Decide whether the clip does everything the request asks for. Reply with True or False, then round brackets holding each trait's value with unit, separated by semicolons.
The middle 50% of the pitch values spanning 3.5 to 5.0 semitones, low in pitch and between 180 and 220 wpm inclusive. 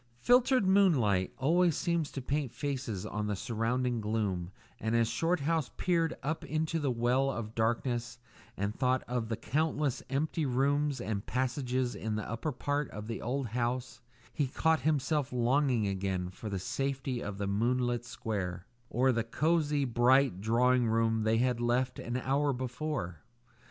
False (4.1 semitones; 125 Hz; 155 wpm)